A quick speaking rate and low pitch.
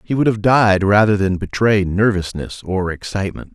No: average, 170 wpm; low, 100 Hz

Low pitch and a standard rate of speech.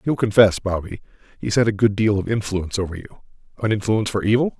Yes: low, 105 Hz; average, 195 wpm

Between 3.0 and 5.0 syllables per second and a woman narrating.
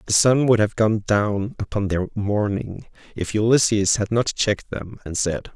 No: 4.5 syllables/s; male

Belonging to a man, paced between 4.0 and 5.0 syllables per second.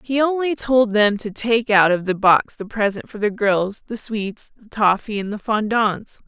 No: female; 4.3 syllables/s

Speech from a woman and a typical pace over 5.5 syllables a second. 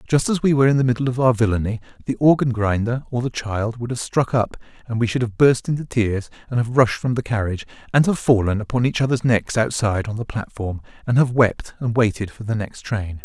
No: male; 5.9 syllables/s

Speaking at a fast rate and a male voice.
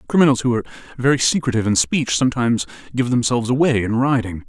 No: average, 175 wpm; male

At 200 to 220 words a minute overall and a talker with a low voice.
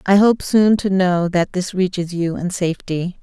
No: fast, 205 wpm; medium, 185 Hz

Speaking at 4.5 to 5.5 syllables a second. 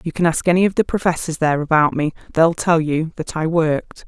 No: 5.9 syllables/s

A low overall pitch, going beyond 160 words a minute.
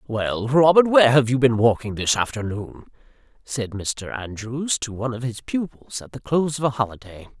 Yes: low, 120 Hz; average, 185 wpm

